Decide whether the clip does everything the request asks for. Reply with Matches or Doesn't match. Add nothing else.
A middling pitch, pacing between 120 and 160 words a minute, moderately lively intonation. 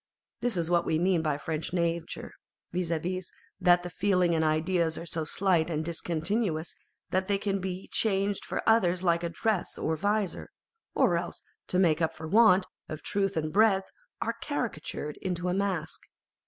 Doesn't match